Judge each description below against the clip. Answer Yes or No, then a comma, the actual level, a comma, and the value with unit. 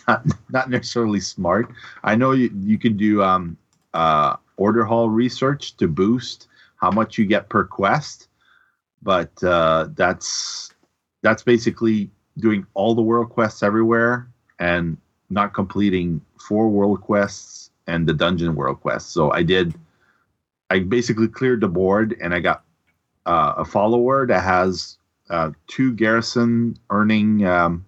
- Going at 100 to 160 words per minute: Yes, average, 140 wpm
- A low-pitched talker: Yes, low, 110 Hz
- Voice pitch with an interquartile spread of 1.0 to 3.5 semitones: No, average, 4.1 semitones